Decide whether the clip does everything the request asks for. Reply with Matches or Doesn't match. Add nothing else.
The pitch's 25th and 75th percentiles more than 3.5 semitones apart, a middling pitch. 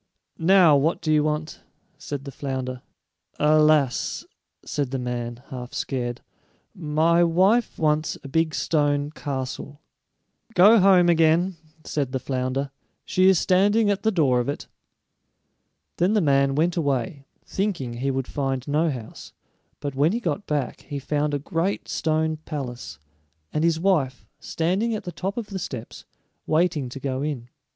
Matches